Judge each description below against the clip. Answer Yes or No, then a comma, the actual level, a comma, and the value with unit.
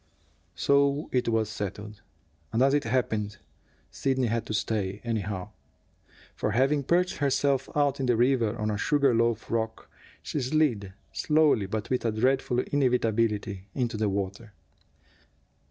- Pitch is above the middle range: No, low, 115 Hz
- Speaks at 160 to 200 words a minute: No, average, 140 wpm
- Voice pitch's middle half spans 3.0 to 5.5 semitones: Yes, average, 4.1 semitones